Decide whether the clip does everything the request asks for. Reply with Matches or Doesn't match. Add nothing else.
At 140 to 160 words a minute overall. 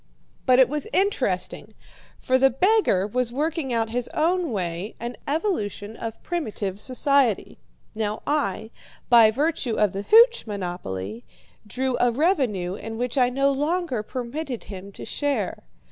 Matches